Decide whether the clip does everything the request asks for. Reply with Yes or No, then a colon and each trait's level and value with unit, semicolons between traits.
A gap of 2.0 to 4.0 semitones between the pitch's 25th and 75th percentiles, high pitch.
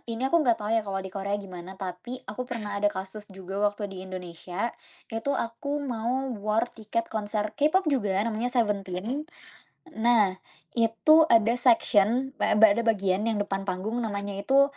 Yes: average, 3.5 semitones; high, 215 Hz